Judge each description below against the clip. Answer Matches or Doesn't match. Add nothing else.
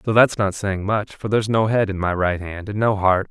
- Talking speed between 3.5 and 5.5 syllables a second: Matches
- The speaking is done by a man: Matches